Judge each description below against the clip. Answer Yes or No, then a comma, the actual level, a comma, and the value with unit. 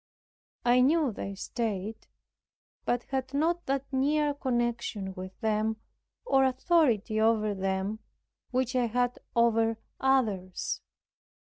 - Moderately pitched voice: No, high, 240 Hz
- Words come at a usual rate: No, slow, 105 wpm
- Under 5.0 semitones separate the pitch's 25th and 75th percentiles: Yes, average, 3.8 semitones